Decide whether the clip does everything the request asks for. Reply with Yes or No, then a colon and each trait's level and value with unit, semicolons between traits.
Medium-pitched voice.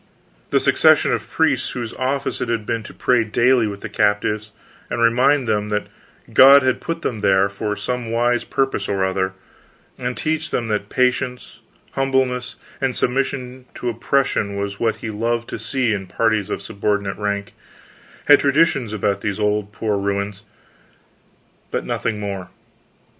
No: low, 115 Hz